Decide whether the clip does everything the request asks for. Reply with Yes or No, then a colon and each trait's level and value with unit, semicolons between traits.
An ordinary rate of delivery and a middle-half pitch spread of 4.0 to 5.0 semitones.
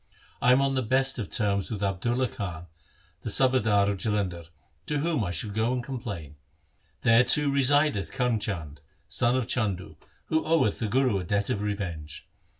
Yes: average, 175 wpm; average, 4.7 semitones